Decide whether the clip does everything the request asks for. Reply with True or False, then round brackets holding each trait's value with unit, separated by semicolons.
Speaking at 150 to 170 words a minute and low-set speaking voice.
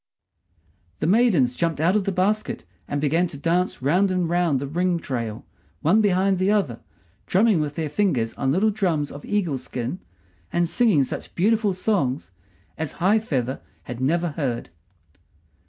False (160 wpm; 170 Hz)